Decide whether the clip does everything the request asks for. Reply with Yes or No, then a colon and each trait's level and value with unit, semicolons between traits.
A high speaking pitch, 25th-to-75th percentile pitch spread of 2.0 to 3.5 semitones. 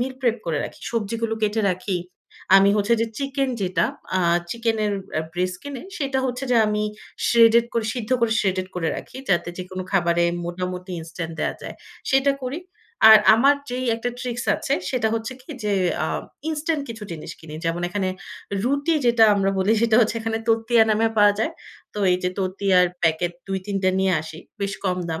No: high, 215 Hz; average, 4.5 semitones